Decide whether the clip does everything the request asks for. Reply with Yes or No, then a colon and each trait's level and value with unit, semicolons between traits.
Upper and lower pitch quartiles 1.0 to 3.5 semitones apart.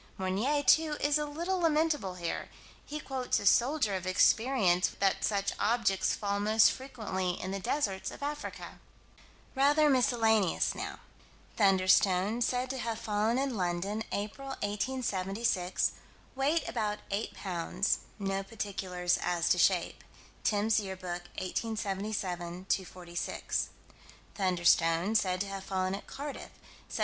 No: average, 5.3 semitones